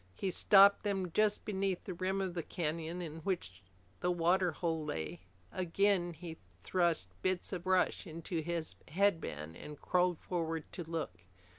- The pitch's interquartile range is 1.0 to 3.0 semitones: Yes, average, 2.7 semitones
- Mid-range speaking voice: Yes, medium, 175 Hz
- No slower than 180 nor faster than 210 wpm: No, average, 155 wpm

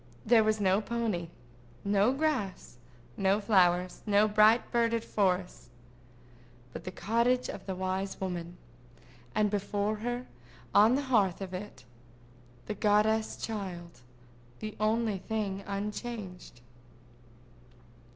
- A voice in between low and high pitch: No, high, 200 Hz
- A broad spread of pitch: No, average, 3.3 semitones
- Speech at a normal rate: No, slow, 105 wpm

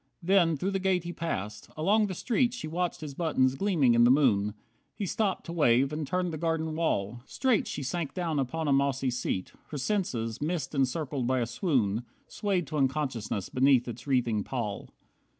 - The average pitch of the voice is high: No, medium, 145 Hz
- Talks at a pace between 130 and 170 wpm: No, average, 185 wpm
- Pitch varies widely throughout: Yes, wide, 5.7 semitones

